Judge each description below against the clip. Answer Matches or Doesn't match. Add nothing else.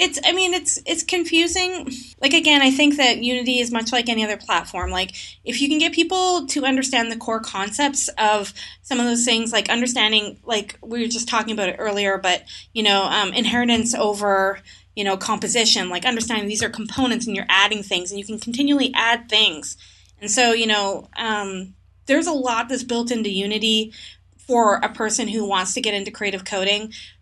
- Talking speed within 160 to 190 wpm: Doesn't match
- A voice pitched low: Doesn't match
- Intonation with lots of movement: Doesn't match